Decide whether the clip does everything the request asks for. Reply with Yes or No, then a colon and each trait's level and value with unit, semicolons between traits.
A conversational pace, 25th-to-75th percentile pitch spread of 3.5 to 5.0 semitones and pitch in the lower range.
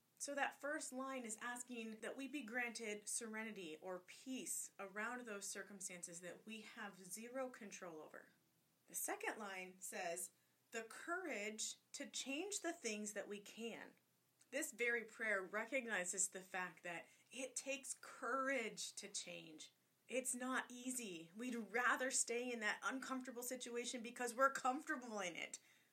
No: average, 145 wpm; average, 4.5 semitones; high, 230 Hz